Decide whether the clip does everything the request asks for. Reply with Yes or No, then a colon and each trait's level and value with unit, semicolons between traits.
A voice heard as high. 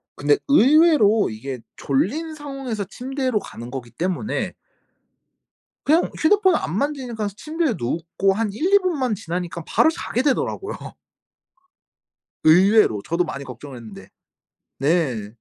Yes: high, 210 Hz